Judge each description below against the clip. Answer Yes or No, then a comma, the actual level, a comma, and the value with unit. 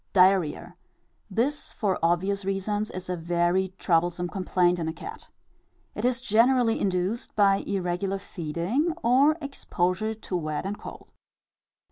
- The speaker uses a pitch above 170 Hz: Yes, high, 190 Hz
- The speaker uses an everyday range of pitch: Yes, average, 3.7 semitones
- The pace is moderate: No, slow, 130 wpm